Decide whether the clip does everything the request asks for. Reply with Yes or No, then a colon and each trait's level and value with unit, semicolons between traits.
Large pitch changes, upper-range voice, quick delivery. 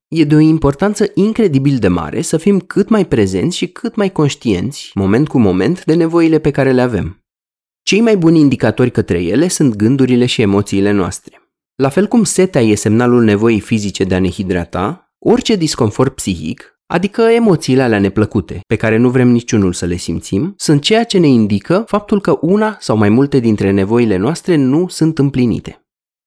No: wide, 8.2 semitones; low, 130 Hz; fast, 185 wpm